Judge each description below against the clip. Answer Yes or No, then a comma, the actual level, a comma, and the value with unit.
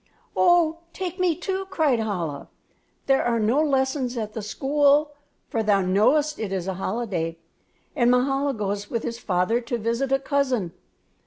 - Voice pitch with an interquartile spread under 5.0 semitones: No, wide, 5.5 semitones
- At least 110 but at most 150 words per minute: No, average, 160 wpm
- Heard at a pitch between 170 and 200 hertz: No, high, 240 Hz